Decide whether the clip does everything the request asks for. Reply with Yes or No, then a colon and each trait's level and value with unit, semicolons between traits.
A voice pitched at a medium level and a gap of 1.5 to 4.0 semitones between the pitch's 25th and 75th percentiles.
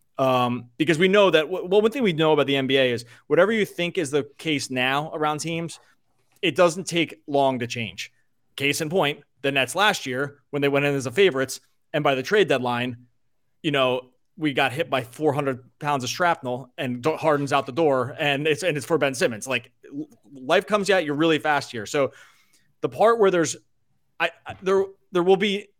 No: medium, 145 Hz; average, 4.4 semitones